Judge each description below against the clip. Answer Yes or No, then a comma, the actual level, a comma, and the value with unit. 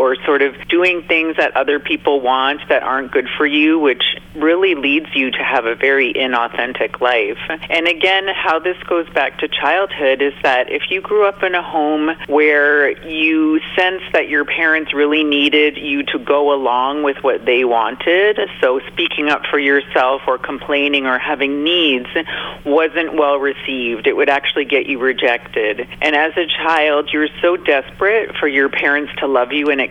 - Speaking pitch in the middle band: Yes, medium, 150 Hz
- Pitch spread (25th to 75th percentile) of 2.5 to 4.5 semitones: Yes, average, 3.2 semitones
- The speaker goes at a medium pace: Yes, average, 185 wpm